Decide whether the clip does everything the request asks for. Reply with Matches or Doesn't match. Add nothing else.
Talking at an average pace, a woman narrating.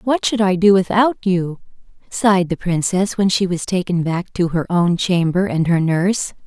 Matches